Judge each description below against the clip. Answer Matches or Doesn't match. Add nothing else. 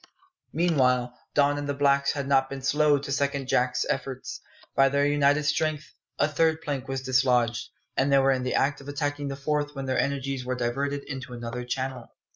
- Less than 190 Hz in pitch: Matches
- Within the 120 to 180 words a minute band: Doesn't match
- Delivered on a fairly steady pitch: Matches